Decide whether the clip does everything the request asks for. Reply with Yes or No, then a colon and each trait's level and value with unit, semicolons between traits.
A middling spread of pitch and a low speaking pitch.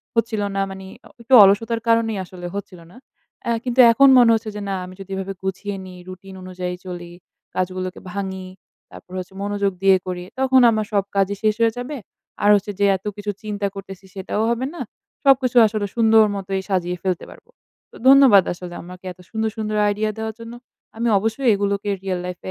No: average, 3.0 semitones; high, 200 Hz